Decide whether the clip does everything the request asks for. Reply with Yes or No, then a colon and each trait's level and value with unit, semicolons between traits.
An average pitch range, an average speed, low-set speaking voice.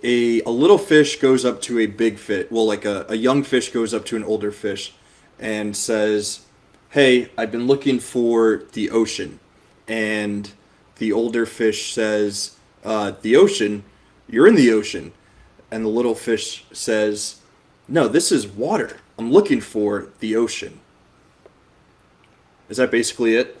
No: narrow, 2.1 semitones; average, 155 wpm; low, 110 Hz